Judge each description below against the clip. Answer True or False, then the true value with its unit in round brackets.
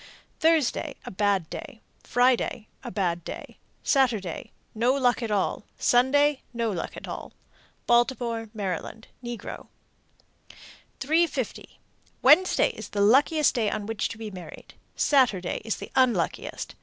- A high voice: True (235 Hz)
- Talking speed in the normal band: False (130 wpm)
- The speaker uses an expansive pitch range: False (4.2 semitones)